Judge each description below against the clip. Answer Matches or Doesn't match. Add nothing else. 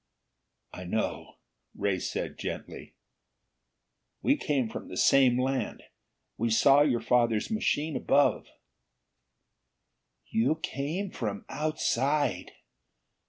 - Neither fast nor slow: Doesn't match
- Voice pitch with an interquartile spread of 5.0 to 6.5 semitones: Doesn't match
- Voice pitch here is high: Doesn't match